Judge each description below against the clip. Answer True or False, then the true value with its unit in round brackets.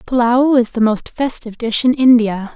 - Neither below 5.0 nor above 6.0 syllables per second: False (4.8 syllables/s)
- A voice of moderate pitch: False (240 Hz)